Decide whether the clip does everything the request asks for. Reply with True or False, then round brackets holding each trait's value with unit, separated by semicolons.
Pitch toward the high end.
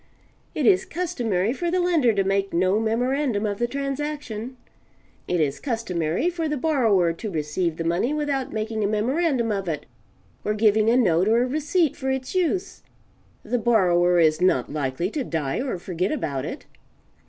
True (225 Hz)